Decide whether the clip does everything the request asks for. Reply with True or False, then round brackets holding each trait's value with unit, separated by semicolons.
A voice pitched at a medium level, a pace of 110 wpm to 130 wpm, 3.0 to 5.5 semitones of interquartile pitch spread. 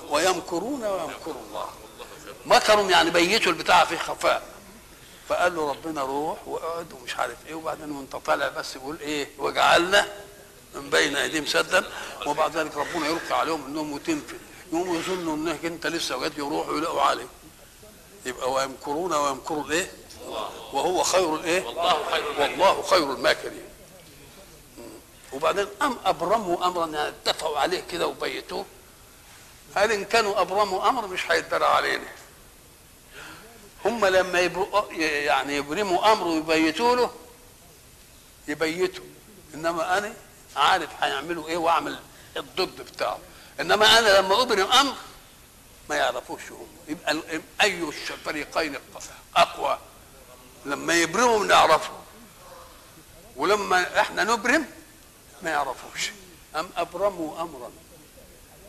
True (175 Hz; 115 wpm; 5.0 semitones)